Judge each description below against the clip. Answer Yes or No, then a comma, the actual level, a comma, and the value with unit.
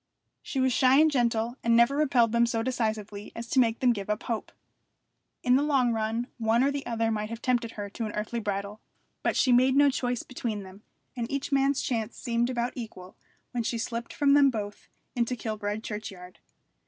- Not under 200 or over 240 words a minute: Yes, fast, 205 wpm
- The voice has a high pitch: Yes, high, 235 Hz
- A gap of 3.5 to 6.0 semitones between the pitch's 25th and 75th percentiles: No, average, 2.7 semitones